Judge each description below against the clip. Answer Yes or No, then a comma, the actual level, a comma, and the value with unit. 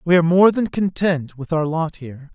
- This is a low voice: No, medium, 165 Hz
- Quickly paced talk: Yes, fast, 230 wpm